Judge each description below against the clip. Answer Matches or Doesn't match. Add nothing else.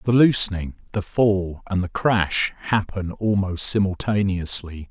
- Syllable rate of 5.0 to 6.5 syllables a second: Doesn't match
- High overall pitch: Doesn't match